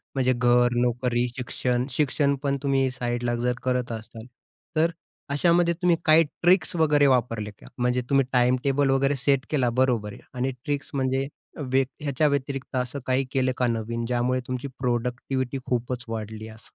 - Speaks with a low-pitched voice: Yes, low, 130 Hz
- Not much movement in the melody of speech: Yes, narrow, 2.3 semitones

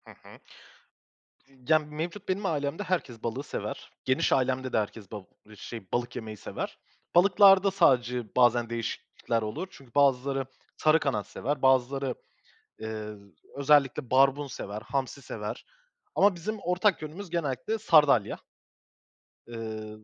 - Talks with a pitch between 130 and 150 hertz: Yes, low, 135 Hz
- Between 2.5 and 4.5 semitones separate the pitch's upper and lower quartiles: No, average, 5.3 semitones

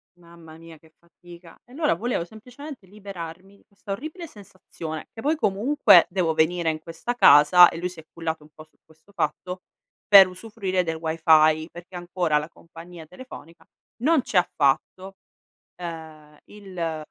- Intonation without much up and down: No, average, 3.7 semitones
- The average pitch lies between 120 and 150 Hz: No, medium, 175 Hz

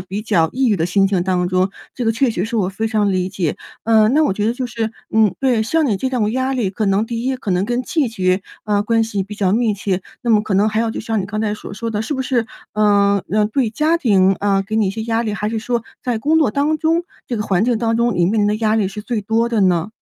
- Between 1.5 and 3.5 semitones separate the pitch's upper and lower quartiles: Yes, average, 3.0 semitones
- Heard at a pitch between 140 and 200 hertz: No, high, 215 Hz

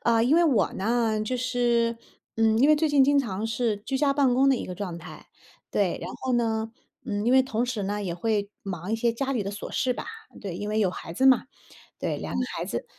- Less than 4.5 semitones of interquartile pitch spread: Yes, average, 3.8 semitones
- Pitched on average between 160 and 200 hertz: No, high, 230 Hz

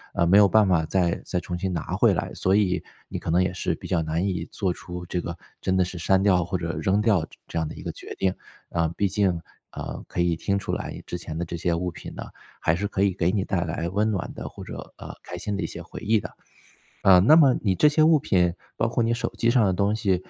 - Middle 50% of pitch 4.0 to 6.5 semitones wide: No, average, 2.8 semitones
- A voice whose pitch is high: No, very low, 95 Hz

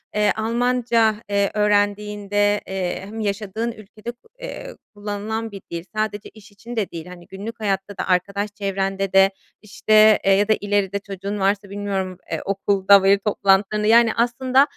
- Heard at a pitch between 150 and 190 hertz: No, high, 205 Hz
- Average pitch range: No, narrow, 1.8 semitones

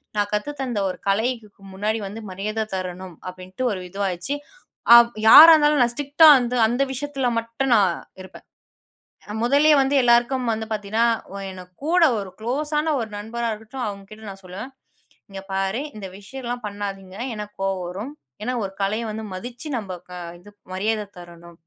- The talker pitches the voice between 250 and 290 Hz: No, high, 215 Hz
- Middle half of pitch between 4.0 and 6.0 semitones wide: Yes, average, 4.5 semitones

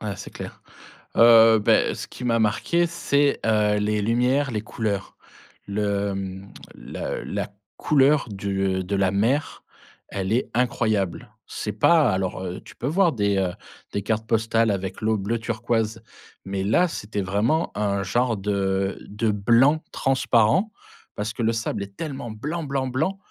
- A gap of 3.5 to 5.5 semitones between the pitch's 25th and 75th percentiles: Yes, average, 3.9 semitones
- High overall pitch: No, low, 110 Hz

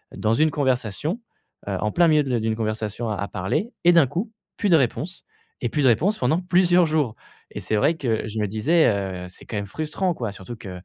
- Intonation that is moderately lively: No, wide, 7.4 semitones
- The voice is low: Yes, low, 125 Hz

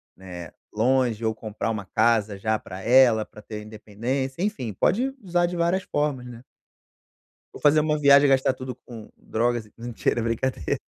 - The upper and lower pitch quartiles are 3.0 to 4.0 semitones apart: No, average, 4.5 semitones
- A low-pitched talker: Yes, low, 120 Hz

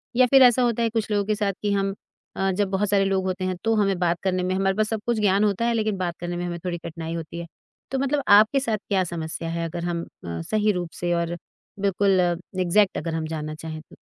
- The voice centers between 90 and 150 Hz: No, high, 190 Hz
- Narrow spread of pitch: No, average, 3.6 semitones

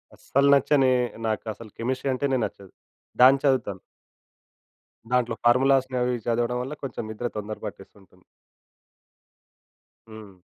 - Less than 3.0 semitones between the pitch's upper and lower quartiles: No, average, 3.3 semitones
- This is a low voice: Yes, low, 125 Hz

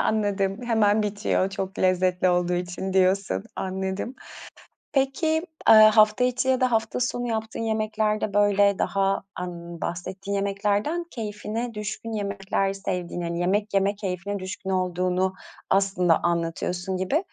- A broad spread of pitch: No, narrow, 2.6 semitones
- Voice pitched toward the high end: Yes, high, 195 Hz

